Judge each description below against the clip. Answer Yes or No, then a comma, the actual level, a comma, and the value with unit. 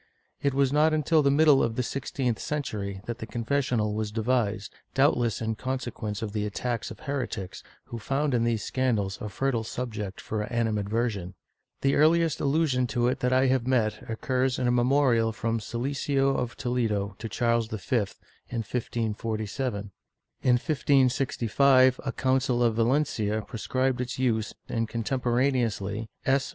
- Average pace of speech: Yes, average, 150 wpm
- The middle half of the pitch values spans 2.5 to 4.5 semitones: Yes, average, 3.2 semitones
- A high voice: No, low, 120 Hz